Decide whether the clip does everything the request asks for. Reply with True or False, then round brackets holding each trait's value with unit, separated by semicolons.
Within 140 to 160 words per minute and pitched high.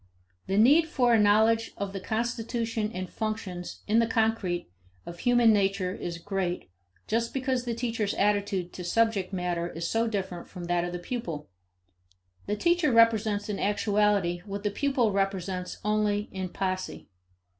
True (155 wpm; 205 Hz)